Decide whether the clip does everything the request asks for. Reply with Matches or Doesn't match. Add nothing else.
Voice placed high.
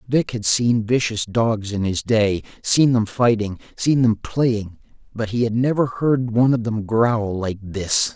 Doesn't match